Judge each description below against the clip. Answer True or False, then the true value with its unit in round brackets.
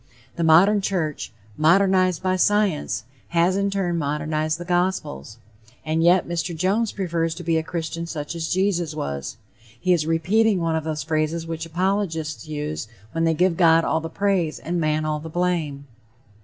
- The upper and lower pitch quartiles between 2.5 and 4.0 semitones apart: True (2.8 semitones)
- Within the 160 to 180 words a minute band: True (170 wpm)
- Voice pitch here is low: False (165 Hz)